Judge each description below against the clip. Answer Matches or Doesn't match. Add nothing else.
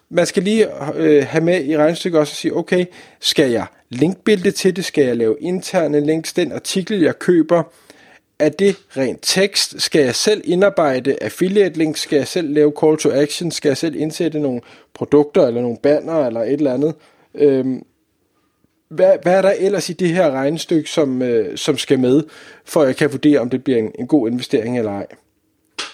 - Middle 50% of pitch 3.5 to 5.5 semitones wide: Matches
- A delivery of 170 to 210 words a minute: Matches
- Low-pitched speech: Doesn't match